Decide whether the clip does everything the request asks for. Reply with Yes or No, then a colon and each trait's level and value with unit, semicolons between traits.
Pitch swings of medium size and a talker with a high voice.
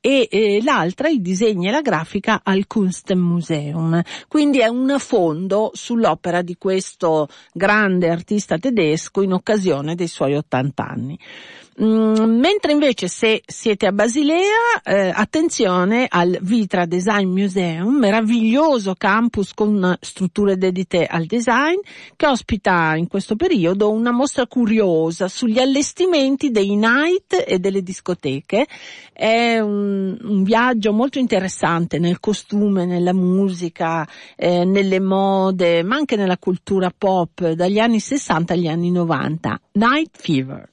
Yes: average, 4.7 semitones; high, 200 Hz